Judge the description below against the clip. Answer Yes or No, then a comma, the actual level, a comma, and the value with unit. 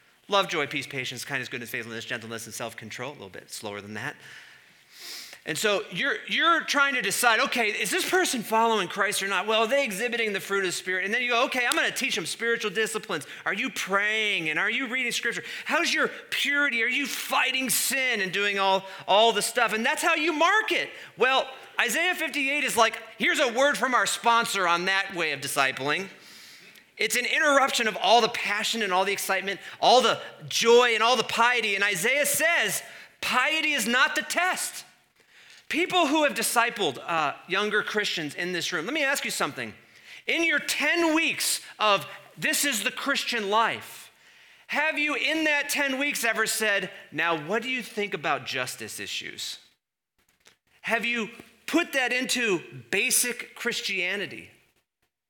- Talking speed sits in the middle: Yes, average, 180 wpm